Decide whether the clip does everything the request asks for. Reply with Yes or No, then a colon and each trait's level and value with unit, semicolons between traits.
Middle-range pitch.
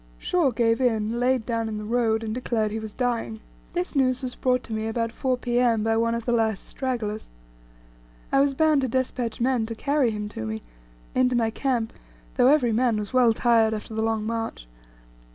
No: high, 230 Hz